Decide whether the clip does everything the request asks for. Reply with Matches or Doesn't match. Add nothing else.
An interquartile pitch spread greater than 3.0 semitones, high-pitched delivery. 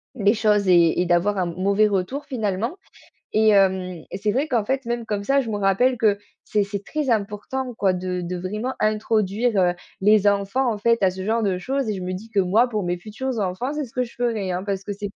Matches